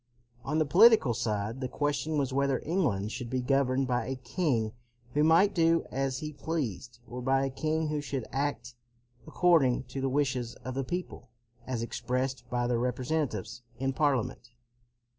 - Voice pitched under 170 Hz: Yes, low, 135 Hz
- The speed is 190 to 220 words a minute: No, average, 165 wpm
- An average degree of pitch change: Yes, average, 3.5 semitones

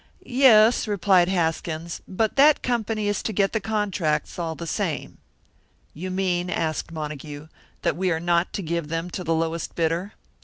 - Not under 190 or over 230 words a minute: No, average, 165 wpm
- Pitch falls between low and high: Yes, medium, 175 Hz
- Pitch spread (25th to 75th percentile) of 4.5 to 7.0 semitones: No, average, 4.0 semitones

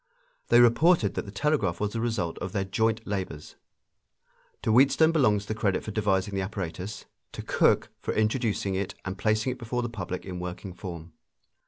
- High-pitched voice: No, low, 105 Hz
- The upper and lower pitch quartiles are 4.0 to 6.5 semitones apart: No, average, 3.5 semitones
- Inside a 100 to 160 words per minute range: No, average, 180 wpm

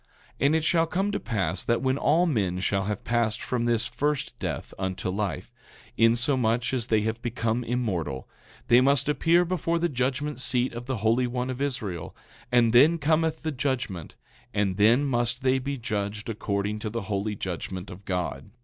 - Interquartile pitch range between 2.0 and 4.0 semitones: No, average, 4.7 semitones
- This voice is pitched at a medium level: No, low, 120 Hz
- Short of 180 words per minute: No, average, 185 wpm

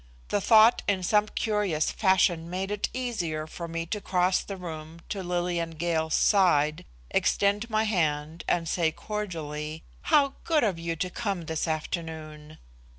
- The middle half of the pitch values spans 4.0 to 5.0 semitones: Yes, average, 4.3 semitones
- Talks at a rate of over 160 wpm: No, average, 150 wpm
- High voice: No, medium, 175 Hz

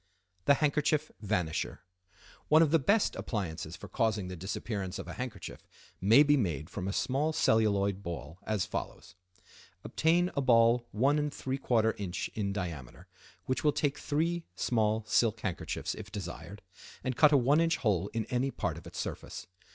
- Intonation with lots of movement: Yes, wide, 6.9 semitones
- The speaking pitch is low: Yes, low, 110 Hz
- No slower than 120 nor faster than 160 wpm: Yes, average, 155 wpm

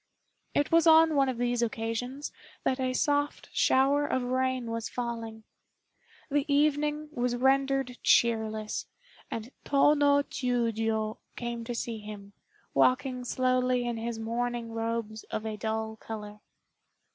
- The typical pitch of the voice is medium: No, high, 245 Hz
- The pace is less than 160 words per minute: Yes, slow, 135 wpm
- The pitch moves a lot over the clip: No, average, 3.2 semitones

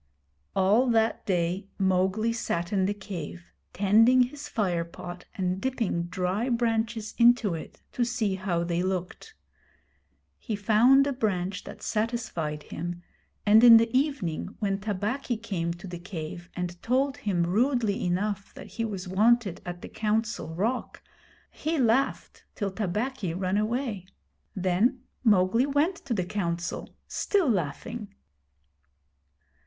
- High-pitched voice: Yes, high, 205 Hz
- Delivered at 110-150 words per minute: Yes, slow, 135 wpm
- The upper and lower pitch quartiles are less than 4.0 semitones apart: No, average, 4.6 semitones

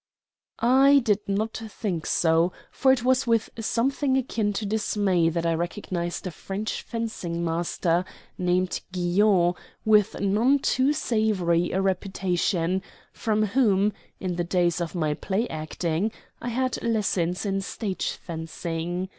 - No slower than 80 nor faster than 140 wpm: Yes, slow, 135 wpm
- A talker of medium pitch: No, high, 195 Hz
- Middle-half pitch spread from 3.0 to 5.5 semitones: Yes, average, 4.2 semitones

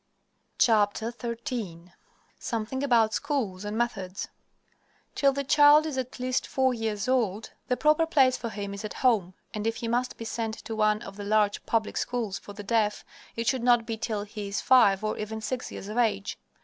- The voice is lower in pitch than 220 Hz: No, high, 225 Hz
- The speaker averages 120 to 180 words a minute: No, average, 190 wpm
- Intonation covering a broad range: No, average, 3.3 semitones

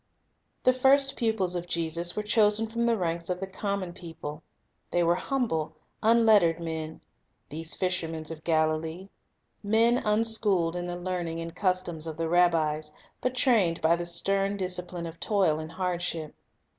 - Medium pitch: Yes, medium, 175 Hz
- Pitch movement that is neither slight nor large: Yes, average, 4.1 semitones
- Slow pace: No, average, 155 wpm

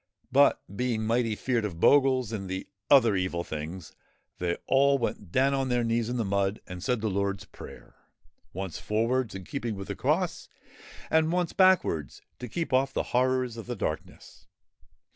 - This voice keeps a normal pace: Yes, average, 175 wpm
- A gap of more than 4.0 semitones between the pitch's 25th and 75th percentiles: Yes, average, 4.9 semitones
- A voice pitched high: No, low, 115 Hz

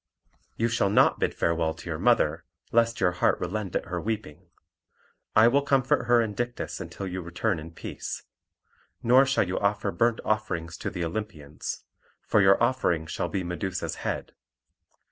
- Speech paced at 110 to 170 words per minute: Yes, average, 165 wpm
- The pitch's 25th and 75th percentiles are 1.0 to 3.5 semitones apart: No, average, 5.0 semitones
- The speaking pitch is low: Yes, low, 100 Hz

